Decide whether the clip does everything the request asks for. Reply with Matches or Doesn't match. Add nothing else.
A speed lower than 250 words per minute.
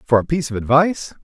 Matches